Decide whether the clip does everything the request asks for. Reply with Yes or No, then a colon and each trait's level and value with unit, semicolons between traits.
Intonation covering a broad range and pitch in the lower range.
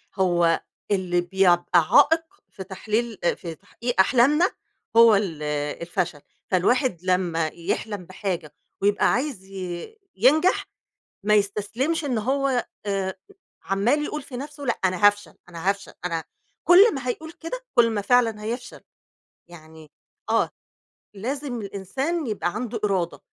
No: wide, 5.7 semitones; high, 205 Hz